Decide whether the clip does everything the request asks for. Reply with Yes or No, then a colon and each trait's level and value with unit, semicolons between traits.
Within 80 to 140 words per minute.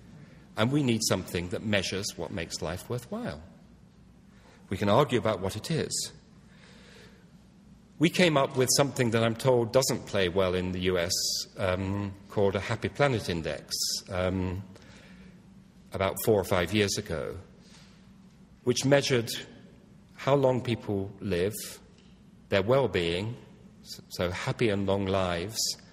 Yes: slow, 135 wpm